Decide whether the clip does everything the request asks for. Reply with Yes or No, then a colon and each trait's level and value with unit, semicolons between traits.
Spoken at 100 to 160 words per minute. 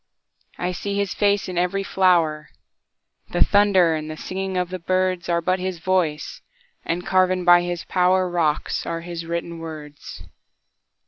Yes: slow, 135 wpm